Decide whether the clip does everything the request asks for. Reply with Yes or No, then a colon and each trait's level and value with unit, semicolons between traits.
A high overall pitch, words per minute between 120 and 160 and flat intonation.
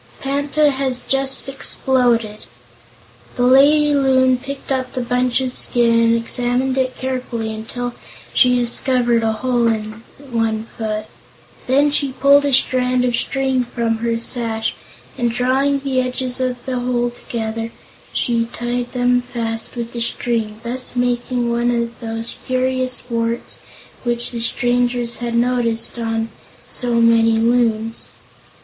Yes: high, 245 Hz; average, 140 wpm; narrow, 1.8 semitones